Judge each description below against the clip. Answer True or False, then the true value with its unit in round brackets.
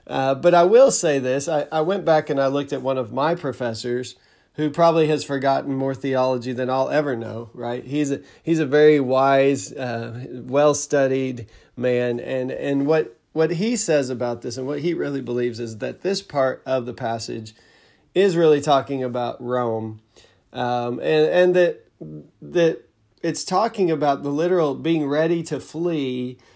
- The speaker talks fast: False (175 wpm)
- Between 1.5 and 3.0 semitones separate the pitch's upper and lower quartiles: False (3.9 semitones)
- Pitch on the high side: False (135 Hz)